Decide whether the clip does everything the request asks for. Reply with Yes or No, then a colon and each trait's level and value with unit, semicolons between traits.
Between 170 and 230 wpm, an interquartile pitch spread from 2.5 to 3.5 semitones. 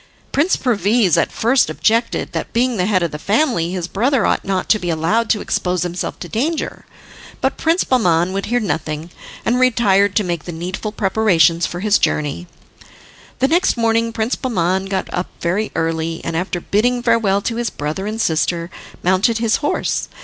No: average, 180 wpm; average, 4.9 semitones